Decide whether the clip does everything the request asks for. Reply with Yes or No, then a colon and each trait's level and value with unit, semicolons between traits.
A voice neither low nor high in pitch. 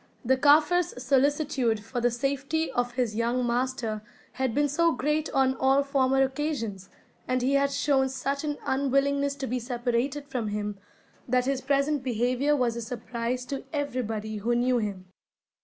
No: very high, 260 Hz